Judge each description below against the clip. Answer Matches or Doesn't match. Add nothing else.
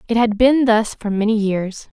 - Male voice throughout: Doesn't match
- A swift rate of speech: Matches